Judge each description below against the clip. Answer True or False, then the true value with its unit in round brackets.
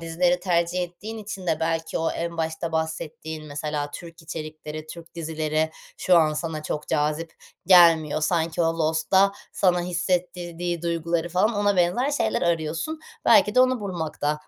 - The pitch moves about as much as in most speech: False (2.0 semitones)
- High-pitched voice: False (165 Hz)